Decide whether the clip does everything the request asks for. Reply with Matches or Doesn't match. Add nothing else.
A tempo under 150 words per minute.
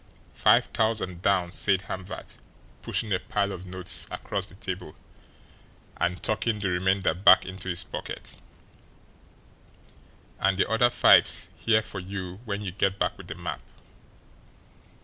Matches